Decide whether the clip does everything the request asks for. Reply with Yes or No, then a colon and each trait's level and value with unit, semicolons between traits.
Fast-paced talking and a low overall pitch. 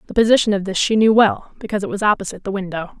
No: fast, 260 wpm; high, 200 Hz